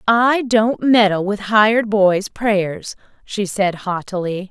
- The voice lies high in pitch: Yes, high, 205 Hz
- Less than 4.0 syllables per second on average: Yes, 3.5 syllables/s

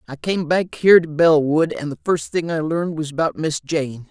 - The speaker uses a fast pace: Yes, fast, 235 wpm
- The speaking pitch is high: No, medium, 155 Hz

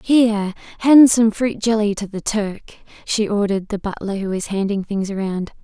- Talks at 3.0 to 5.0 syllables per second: Yes, 4.9 syllables/s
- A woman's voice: Yes, female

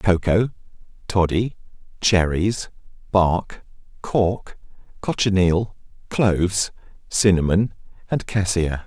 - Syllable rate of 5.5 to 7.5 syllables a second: No, 3.4 syllables/s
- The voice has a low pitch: Yes, very low, 95 Hz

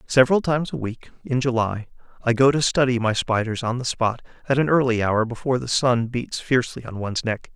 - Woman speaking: No, male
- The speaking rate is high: Yes, fast, 215 wpm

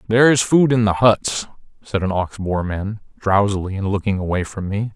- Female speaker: No, male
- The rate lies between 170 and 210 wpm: Yes, fast, 205 wpm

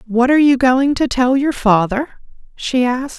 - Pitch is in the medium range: No, very high, 255 Hz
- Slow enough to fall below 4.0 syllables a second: No, 4.8 syllables/s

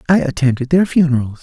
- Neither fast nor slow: Yes, average, 170 wpm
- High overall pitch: No, medium, 145 Hz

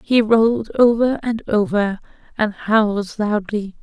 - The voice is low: No, high, 215 Hz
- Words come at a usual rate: No, slow, 125 wpm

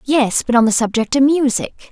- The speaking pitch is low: No, very high, 255 Hz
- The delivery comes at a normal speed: No, fast, 220 wpm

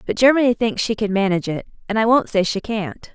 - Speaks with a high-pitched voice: Yes, high, 215 Hz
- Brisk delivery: Yes, fast, 250 wpm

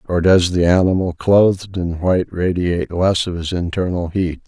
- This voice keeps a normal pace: Yes, average, 175 wpm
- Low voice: Yes, very low, 90 Hz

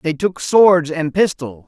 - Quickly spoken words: No, average, 180 wpm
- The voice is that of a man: Yes, male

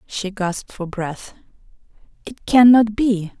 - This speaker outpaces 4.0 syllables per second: No, 3.9 syllables/s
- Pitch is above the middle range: Yes, high, 205 Hz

